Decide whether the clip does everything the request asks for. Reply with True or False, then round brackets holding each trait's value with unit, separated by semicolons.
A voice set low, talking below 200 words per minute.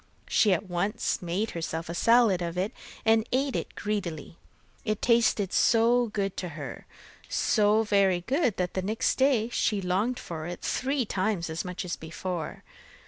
False (200 Hz; 165 wpm)